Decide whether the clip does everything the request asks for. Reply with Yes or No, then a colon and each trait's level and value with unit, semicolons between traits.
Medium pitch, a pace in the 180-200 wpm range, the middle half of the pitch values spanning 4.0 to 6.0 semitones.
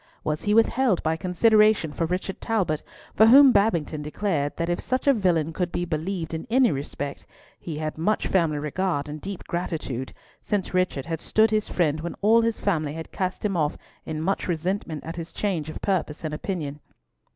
Yes: medium, 175 Hz; average, 190 wpm; average, 4.6 semitones